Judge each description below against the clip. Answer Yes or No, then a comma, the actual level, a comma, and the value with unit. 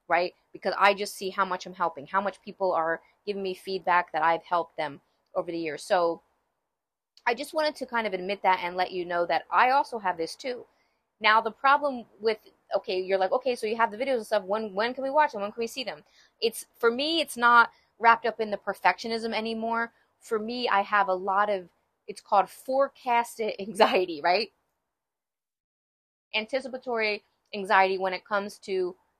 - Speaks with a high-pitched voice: Yes, high, 210 Hz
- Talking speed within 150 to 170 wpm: No, average, 200 wpm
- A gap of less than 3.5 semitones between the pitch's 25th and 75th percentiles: No, average, 4.1 semitones